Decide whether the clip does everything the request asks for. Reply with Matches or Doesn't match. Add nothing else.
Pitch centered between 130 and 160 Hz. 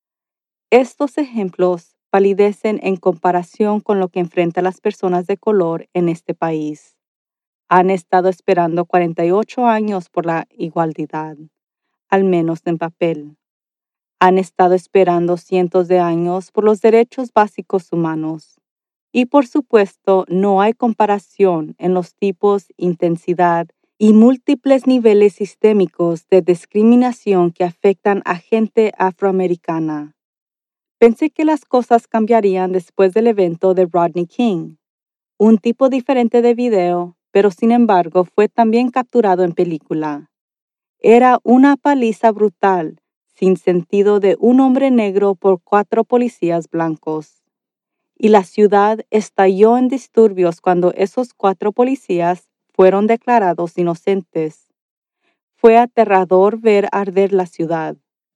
Doesn't match